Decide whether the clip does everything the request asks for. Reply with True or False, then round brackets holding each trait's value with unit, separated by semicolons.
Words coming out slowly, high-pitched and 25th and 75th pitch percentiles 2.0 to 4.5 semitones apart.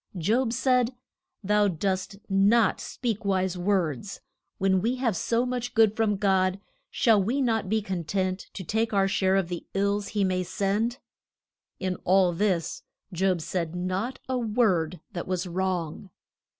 False (155 wpm; 195 Hz; 3.2 semitones)